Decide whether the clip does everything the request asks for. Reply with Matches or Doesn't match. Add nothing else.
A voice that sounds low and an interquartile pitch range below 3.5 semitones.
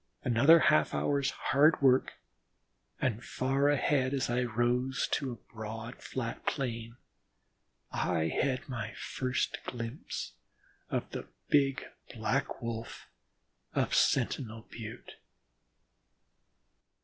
Matches